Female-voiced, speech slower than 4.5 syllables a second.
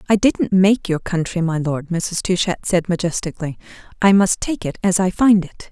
No: female; 5.1 syllables/s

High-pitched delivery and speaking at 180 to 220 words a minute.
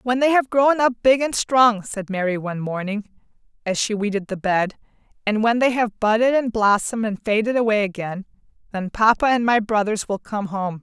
Yes: high, 220 Hz; average, 200 wpm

